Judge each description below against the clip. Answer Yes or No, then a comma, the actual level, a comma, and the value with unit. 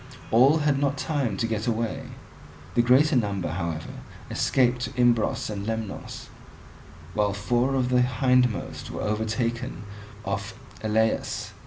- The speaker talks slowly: Yes, slow, 130 wpm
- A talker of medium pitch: No, low, 115 Hz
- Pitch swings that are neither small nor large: Yes, average, 3.0 semitones